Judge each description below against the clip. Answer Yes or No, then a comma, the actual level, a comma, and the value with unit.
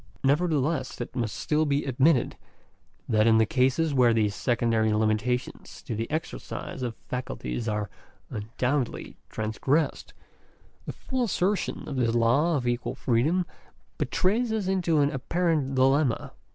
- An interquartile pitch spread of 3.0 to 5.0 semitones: No, wide, 5.4 semitones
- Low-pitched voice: Yes, low, 130 Hz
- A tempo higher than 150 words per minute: No, slow, 135 wpm